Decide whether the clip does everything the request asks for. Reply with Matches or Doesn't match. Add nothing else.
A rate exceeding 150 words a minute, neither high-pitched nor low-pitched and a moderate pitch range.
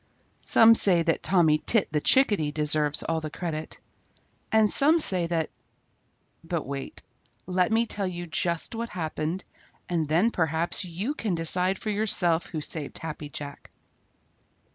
Doesn't match